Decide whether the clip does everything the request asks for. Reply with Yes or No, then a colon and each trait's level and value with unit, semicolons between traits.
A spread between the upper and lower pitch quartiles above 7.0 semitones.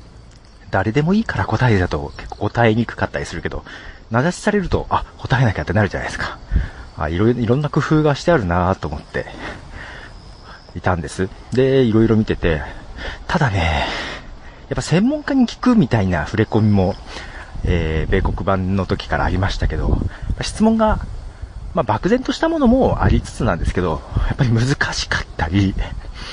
No: wide, 6.7 semitones